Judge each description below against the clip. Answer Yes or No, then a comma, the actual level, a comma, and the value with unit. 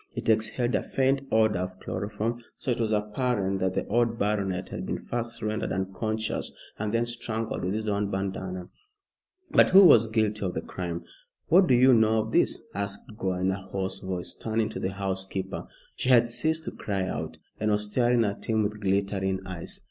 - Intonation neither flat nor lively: Yes, average, 3.2 semitones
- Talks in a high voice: No, low, 105 Hz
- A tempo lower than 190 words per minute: No, average, 195 wpm